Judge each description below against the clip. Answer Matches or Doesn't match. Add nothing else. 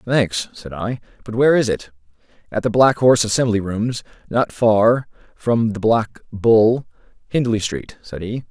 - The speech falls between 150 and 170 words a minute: Matches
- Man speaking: Matches